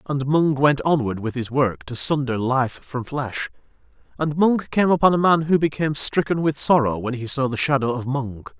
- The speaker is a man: Yes, male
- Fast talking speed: Yes, fast, 210 wpm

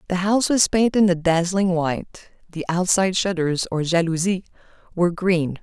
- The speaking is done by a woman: Yes, female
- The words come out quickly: No, average, 150 wpm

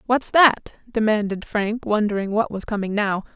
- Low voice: No, high, 215 Hz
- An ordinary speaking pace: Yes, average, 160 wpm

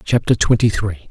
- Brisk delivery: No, average, 160 wpm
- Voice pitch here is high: No, low, 110 Hz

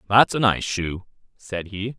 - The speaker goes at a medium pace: Yes, average, 180 wpm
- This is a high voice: No, low, 105 Hz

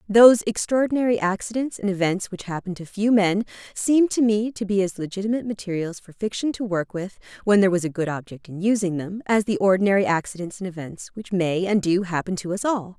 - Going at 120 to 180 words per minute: No, fast, 205 wpm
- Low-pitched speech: No, high, 200 Hz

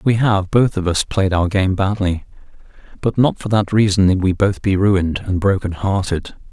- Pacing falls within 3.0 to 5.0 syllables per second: Yes, 4.9 syllables/s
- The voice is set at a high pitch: No, low, 100 Hz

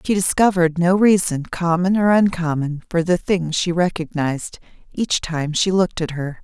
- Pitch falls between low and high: Yes, medium, 175 Hz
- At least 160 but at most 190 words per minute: Yes, average, 175 wpm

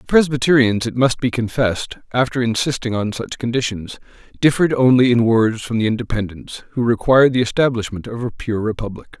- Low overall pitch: Yes, low, 120 Hz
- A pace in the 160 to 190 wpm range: Yes, average, 170 wpm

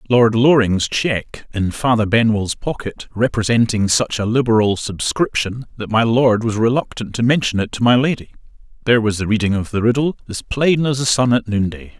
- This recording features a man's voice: Yes, male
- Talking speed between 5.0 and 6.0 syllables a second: Yes, 5.2 syllables/s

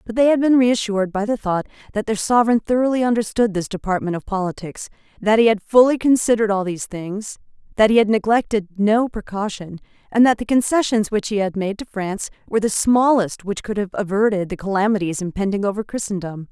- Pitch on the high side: Yes, high, 210 Hz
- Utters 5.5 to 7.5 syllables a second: Yes, 6.0 syllables/s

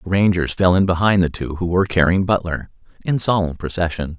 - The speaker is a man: Yes, male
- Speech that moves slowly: No, average, 200 wpm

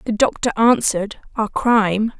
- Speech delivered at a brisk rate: No, slow, 135 wpm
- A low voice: No, high, 220 Hz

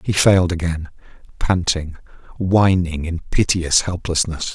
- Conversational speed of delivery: No, slow, 105 wpm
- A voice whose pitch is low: Yes, very low, 90 Hz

